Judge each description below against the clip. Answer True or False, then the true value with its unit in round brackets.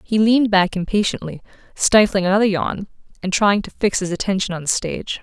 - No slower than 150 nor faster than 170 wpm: False (185 wpm)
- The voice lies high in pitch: True (195 Hz)